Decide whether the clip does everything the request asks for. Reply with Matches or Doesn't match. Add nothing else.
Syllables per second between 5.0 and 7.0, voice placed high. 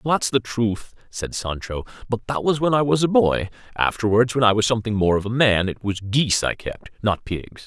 Doesn't match